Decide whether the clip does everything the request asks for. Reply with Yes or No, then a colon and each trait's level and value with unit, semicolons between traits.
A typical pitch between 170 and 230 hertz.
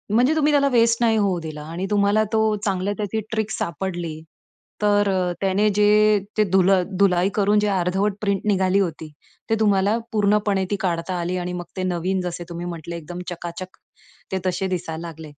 Yes: high, 190 Hz